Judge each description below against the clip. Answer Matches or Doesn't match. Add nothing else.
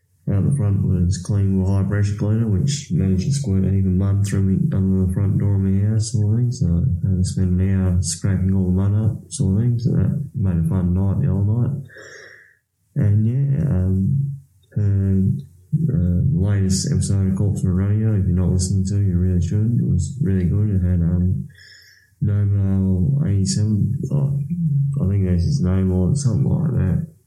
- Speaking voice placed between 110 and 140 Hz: Doesn't match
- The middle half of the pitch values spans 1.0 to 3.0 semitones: Doesn't match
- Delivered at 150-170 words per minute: Doesn't match